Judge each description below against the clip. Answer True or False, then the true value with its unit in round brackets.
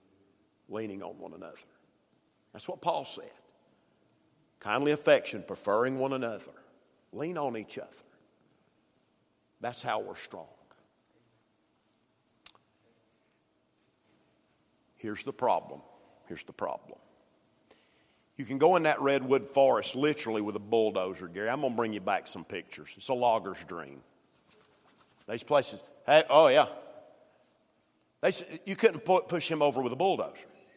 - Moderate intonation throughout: False (6.6 semitones)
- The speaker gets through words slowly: True (125 wpm)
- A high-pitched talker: False (135 Hz)